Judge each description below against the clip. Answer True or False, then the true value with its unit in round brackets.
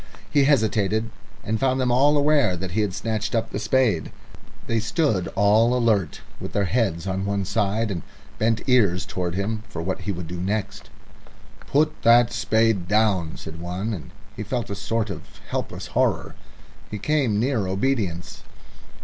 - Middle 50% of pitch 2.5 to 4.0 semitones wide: True (3.4 semitones)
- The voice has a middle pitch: False (105 Hz)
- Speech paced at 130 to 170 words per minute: True (165 wpm)